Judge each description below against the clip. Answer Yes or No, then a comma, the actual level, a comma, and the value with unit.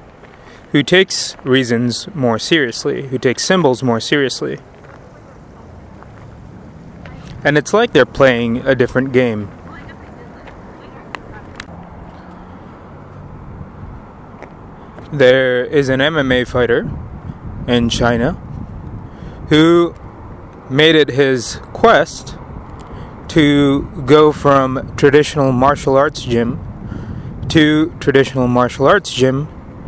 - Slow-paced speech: Yes, slow, 85 wpm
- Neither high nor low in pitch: No, low, 130 Hz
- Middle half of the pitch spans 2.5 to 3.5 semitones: Yes, average, 3.2 semitones